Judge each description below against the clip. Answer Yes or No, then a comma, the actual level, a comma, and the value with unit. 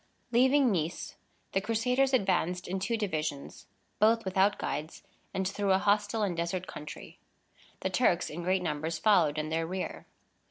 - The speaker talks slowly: No, average, 155 wpm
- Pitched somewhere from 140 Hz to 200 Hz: Yes, high, 190 Hz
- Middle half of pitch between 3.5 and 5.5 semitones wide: Yes, average, 4.4 semitones